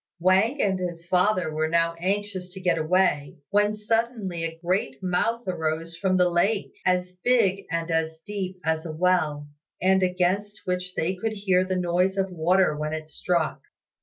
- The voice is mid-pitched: Yes, medium, 180 Hz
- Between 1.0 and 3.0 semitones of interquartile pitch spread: Yes, narrow, 2.6 semitones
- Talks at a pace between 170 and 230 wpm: Yes, average, 175 wpm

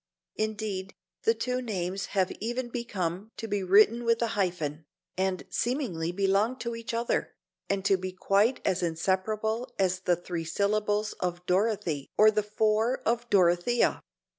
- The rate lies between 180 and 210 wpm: No, average, 155 wpm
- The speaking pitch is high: Yes, high, 205 Hz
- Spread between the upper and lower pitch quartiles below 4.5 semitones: Yes, average, 3.7 semitones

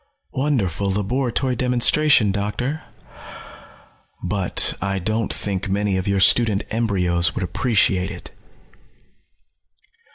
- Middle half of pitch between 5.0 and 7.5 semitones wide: No, average, 4.0 semitones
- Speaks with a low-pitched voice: Yes, low, 105 Hz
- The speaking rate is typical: No, slow, 95 wpm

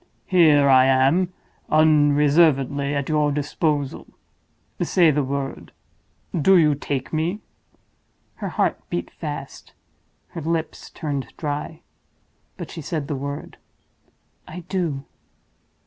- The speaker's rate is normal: No, slow, 100 wpm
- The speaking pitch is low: No, medium, 150 Hz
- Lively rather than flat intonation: No, narrow, 2.6 semitones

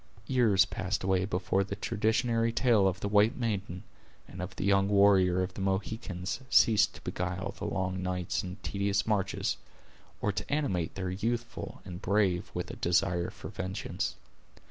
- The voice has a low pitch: Yes, very low, 95 Hz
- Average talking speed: Yes, average, 165 wpm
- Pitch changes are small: Yes, narrow, 2.2 semitones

